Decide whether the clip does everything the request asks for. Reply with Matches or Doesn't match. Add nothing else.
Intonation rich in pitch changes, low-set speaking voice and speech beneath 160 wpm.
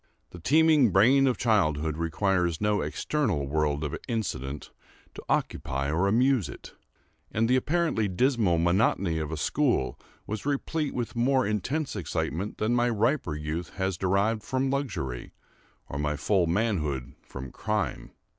Matches